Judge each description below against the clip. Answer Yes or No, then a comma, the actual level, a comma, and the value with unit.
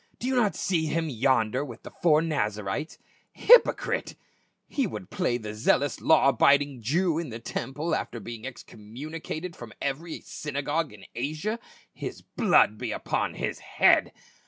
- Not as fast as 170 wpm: Yes, average, 160 wpm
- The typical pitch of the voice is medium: Yes, medium, 145 Hz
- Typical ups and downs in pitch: No, wide, 5.7 semitones